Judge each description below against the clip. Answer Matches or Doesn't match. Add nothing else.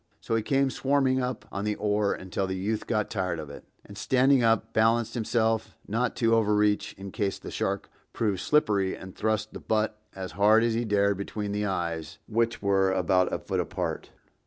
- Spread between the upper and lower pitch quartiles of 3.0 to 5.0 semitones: Doesn't match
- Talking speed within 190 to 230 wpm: Matches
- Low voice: Matches